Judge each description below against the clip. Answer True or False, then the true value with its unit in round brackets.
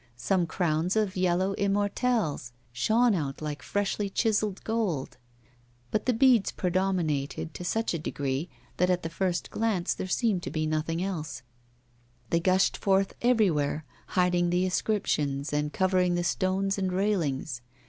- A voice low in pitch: False (180 Hz)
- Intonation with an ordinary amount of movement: True (4.2 semitones)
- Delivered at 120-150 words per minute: True (145 wpm)